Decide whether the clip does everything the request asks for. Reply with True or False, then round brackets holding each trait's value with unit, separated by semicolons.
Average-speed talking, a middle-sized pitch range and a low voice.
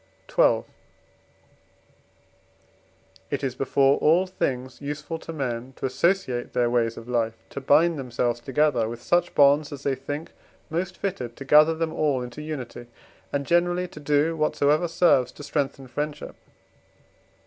False (145 wpm; 4.0 semitones; 145 Hz)